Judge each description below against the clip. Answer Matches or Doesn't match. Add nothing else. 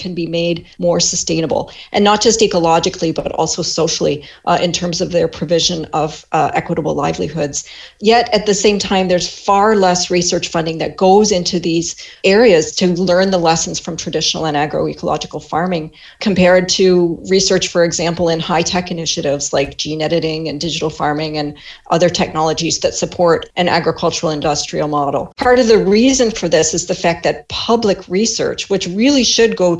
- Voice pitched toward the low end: Doesn't match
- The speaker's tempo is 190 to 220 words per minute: Doesn't match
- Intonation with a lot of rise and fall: Doesn't match